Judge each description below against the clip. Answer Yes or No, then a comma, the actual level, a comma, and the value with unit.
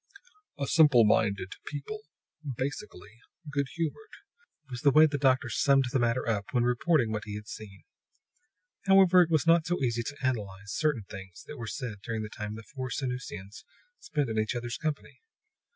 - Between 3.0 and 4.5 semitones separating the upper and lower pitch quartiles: No, wide, 5.4 semitones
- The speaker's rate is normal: Yes, average, 175 wpm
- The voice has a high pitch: No, low, 125 Hz